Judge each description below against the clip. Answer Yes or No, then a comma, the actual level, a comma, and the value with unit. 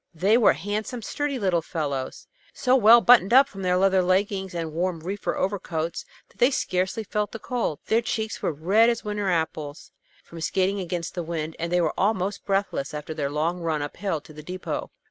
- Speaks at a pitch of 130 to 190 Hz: Yes, medium, 185 Hz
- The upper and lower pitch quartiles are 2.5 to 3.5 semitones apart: No, average, 4.3 semitones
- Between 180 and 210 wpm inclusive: Yes, average, 200 wpm